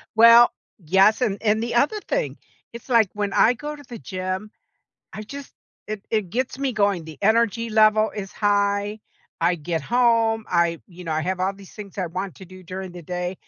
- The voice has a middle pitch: No, high, 205 Hz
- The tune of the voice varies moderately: Yes, average, 3.7 semitones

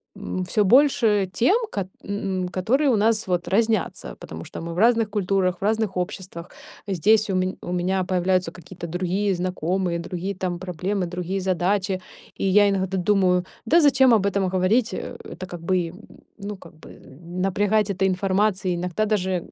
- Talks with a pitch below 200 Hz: Yes, high, 190 Hz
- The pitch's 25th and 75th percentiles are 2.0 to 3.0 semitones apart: Yes, narrow, 2.4 semitones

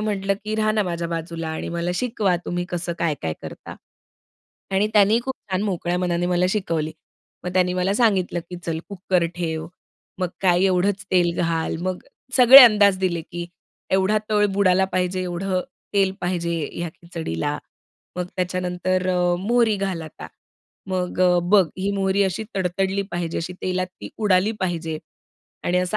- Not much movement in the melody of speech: Yes, narrow, 2.0 semitones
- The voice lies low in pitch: No, medium, 180 Hz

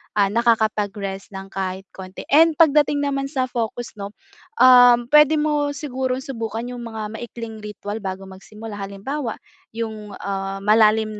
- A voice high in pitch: Yes, high, 225 Hz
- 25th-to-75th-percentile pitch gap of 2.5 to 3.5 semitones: No, average, 4.3 semitones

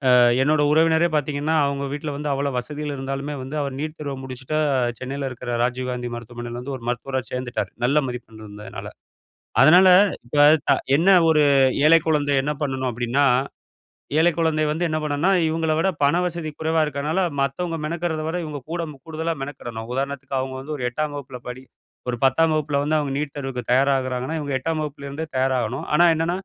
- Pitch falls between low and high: Yes, medium, 145 Hz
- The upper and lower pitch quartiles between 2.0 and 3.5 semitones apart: Yes, average, 3.1 semitones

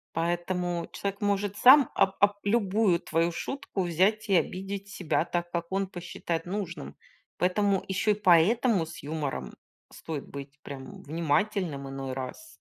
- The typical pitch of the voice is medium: Yes, medium, 180 Hz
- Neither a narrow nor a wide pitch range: Yes, average, 3.7 semitones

